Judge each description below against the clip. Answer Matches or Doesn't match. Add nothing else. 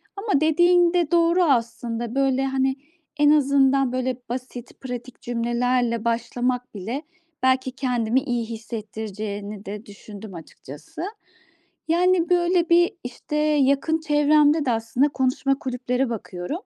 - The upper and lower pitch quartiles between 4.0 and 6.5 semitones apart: Matches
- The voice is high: Matches